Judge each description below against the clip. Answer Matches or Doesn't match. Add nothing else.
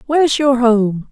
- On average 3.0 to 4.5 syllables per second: Matches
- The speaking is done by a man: Doesn't match